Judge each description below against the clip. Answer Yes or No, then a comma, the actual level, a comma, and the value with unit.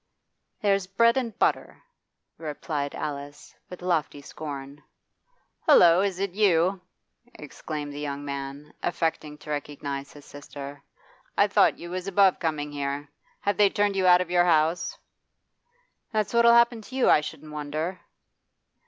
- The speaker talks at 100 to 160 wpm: Yes, average, 145 wpm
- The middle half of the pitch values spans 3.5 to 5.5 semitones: Yes, average, 4.9 semitones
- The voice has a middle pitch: Yes, medium, 160 Hz